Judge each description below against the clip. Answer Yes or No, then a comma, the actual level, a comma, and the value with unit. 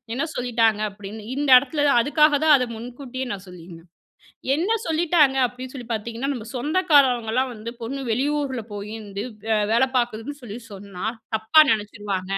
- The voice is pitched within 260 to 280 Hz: No, high, 245 Hz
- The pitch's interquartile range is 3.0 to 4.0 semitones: No, average, 4.8 semitones